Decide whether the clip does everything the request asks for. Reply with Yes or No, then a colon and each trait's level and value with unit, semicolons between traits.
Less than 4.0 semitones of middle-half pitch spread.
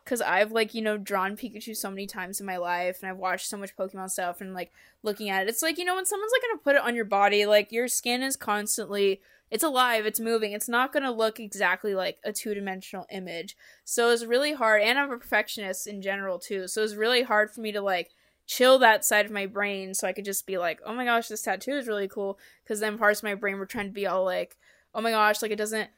Yes: average, 2.8 semitones